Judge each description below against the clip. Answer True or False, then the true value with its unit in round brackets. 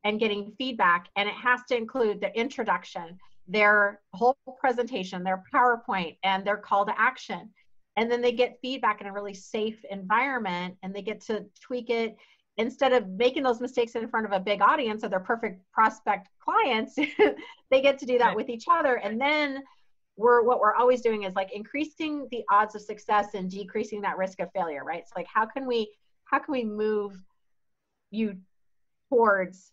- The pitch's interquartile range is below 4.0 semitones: True (3.6 semitones)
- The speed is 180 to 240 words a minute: True (185 wpm)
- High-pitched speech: True (220 Hz)